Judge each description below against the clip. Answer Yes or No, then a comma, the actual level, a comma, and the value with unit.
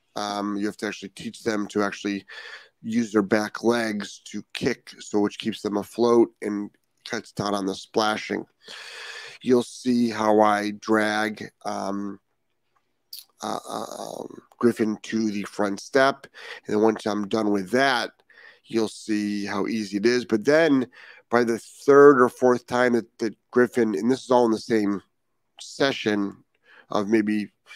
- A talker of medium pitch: No, low, 110 Hz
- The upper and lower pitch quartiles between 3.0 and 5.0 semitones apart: No, narrow, 2.5 semitones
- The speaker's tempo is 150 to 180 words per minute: Yes, average, 160 wpm